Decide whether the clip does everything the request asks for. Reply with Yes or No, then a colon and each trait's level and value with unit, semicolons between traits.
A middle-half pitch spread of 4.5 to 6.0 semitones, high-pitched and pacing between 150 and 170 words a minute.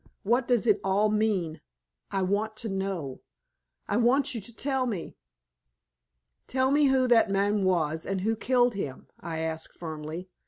Yes: average, 5.2 semitones; high, 205 Hz; average, 160 wpm